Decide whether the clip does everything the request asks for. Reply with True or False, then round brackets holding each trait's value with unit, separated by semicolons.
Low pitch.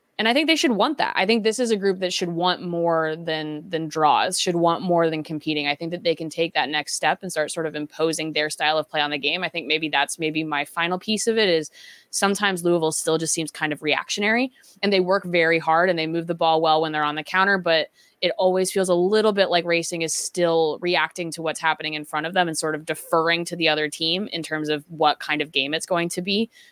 False (165 Hz)